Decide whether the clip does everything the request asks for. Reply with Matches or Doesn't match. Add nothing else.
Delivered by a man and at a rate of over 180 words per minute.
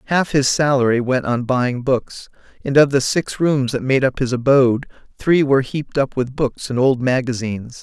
Matches